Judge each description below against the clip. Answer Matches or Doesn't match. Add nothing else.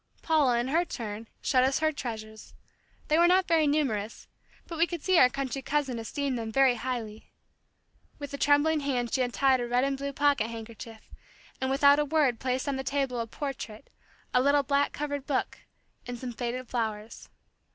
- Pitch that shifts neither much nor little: Matches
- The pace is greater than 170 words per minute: Matches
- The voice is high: Matches